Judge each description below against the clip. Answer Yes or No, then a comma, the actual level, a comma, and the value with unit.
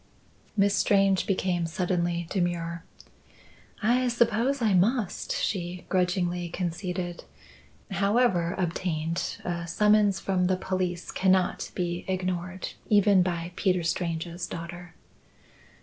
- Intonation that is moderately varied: No, narrow, 2.1 semitones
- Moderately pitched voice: Yes, medium, 180 Hz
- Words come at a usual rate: No, slow, 100 wpm